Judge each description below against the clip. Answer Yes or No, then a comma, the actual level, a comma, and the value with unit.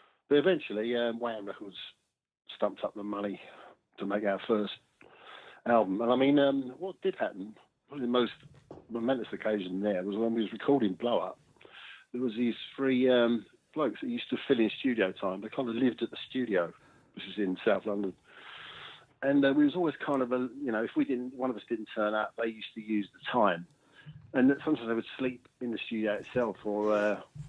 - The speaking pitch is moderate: No, low, 120 Hz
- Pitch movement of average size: Yes, average, 4.0 semitones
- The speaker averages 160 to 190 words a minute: No, fast, 205 wpm